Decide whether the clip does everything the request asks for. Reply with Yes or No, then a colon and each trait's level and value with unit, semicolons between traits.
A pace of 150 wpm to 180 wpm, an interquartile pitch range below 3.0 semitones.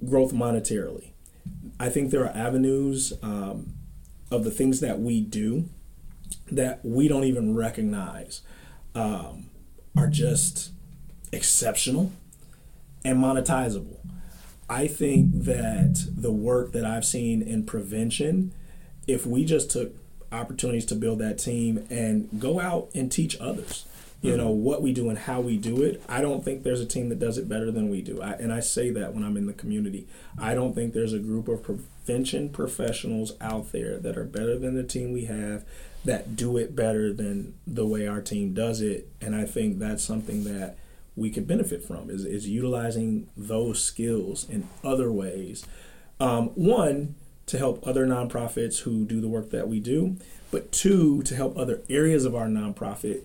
No: average, 170 wpm; average, 4.7 semitones